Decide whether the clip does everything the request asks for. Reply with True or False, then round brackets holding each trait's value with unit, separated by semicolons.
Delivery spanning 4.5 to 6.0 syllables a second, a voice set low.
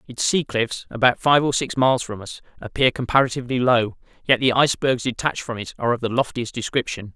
False (6.2 syllables/s; 125 Hz)